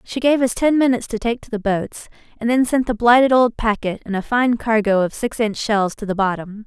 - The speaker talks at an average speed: No, fast, 245 wpm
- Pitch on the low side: No, high, 225 Hz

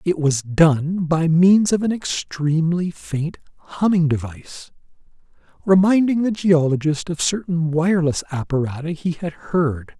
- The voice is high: No, medium, 165 Hz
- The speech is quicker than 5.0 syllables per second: No, 4.4 syllables/s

